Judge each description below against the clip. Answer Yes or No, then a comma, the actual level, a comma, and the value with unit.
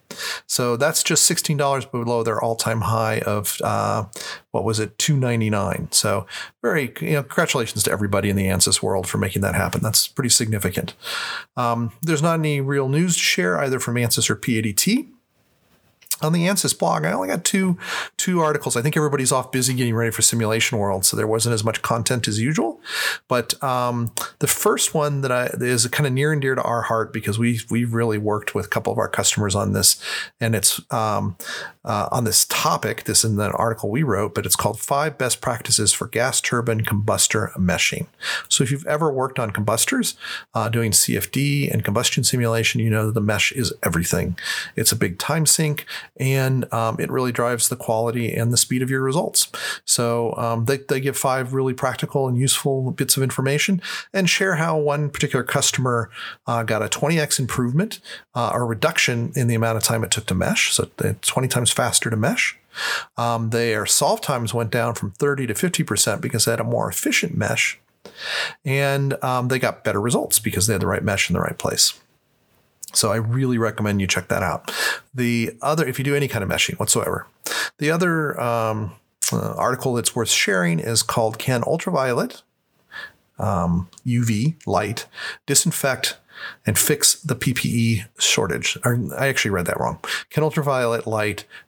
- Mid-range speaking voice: No, low, 120 Hz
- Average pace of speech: Yes, average, 190 wpm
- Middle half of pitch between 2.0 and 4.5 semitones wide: Yes, average, 3.9 semitones